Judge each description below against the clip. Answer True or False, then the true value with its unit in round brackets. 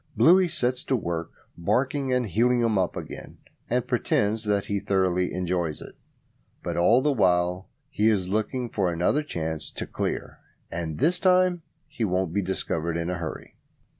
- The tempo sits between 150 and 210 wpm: True (170 wpm)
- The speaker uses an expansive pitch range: True (6.2 semitones)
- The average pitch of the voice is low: True (100 Hz)